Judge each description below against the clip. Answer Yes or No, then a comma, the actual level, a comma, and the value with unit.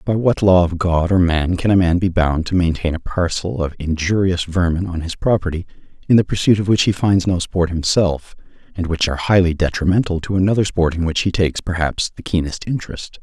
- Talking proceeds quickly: Yes, fast, 220 wpm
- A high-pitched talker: No, very low, 90 Hz